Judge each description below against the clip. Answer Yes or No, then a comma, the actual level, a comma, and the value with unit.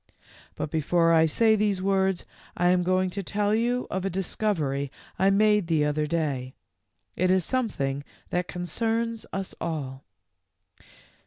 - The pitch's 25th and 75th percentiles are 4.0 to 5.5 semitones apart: Yes, average, 4.6 semitones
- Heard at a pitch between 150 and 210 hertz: Yes, medium, 185 Hz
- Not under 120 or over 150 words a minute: Yes, average, 145 wpm